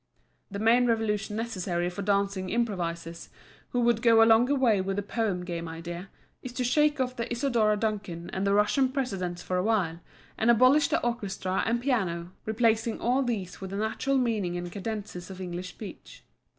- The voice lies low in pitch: No, high, 210 Hz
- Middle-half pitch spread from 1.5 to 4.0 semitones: No, average, 4.4 semitones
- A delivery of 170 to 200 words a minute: Yes, average, 180 wpm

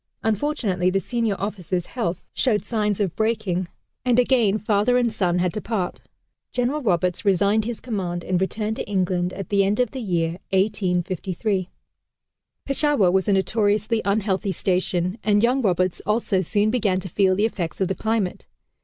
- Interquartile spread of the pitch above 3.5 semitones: No, average, 3.1 semitones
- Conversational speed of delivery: Yes, average, 165 wpm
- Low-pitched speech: No, high, 200 Hz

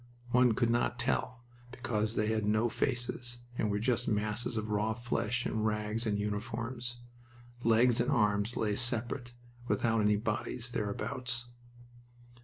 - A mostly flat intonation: Yes, narrow, 2.1 semitones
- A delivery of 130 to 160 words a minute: Yes, average, 140 wpm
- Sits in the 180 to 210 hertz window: No, low, 115 Hz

